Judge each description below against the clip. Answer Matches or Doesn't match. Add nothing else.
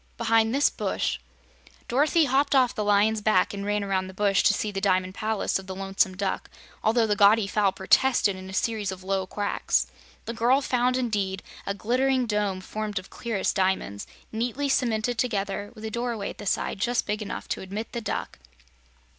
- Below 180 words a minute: Doesn't match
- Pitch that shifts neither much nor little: Matches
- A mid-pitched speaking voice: Doesn't match